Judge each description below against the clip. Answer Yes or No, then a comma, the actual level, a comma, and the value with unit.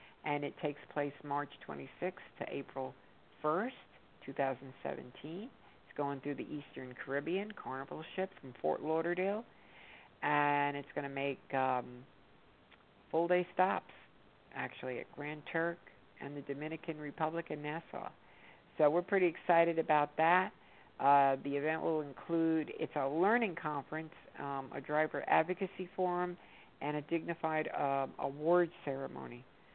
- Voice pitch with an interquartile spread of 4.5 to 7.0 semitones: No, average, 3.3 semitones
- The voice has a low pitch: No, medium, 150 Hz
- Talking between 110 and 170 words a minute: Yes, slow, 135 wpm